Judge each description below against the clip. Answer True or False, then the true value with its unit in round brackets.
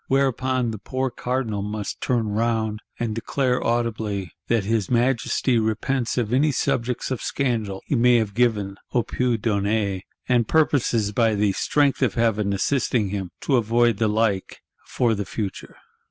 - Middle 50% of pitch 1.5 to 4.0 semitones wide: True (3.0 semitones)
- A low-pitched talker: True (115 Hz)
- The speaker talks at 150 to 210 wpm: True (155 wpm)